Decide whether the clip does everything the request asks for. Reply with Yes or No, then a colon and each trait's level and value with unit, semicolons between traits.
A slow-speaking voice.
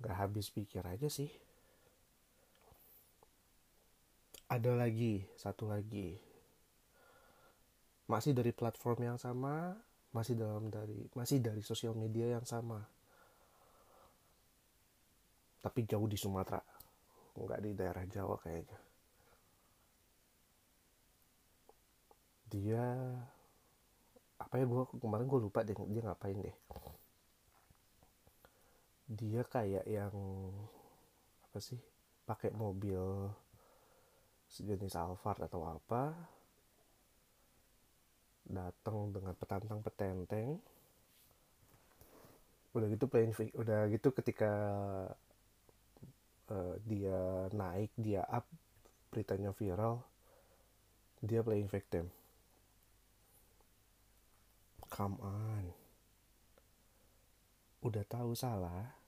Yes: slow, 80 wpm